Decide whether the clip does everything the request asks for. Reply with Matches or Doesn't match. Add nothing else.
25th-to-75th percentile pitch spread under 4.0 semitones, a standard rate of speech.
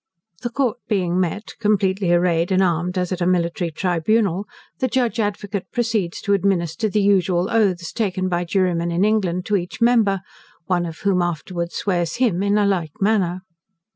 Matches